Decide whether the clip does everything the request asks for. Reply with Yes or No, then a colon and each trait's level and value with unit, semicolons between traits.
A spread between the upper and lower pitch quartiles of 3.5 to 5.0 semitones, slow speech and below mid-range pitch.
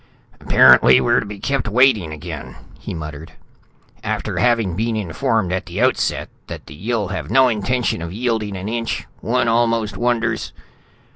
No: average, 4.3 semitones; average, 155 wpm; low, 110 Hz